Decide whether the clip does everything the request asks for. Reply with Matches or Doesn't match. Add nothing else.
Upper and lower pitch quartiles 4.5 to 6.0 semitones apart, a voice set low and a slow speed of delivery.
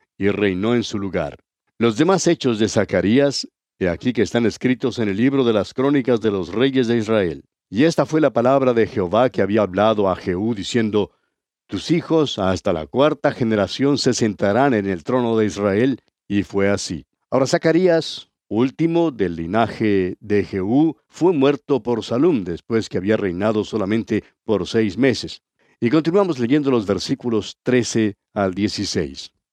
Doesn't match